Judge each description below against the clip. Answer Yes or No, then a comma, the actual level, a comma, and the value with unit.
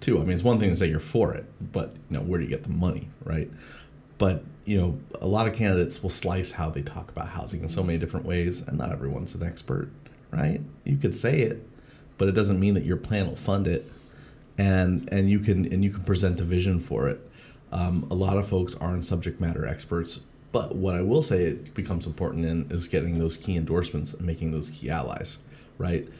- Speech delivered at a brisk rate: Yes, fast, 230 wpm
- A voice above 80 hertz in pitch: Yes, very low, 90 Hz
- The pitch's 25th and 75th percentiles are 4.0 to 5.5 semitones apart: No, average, 2.7 semitones